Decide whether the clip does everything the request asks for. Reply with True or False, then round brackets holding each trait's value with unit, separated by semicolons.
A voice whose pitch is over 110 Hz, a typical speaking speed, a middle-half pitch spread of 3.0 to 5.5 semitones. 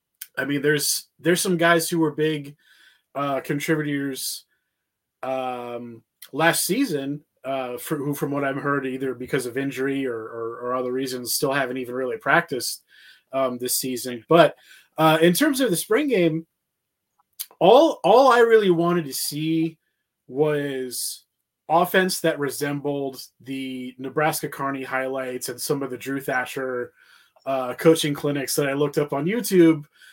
True (140 Hz; 150 wpm; 3.4 semitones)